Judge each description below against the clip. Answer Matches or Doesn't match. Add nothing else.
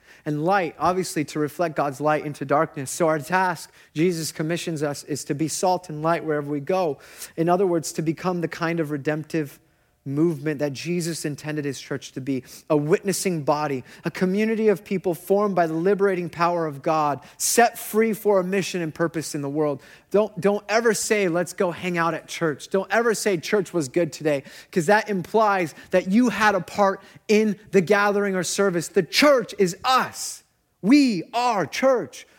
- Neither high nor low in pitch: Matches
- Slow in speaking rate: Doesn't match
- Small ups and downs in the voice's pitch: Doesn't match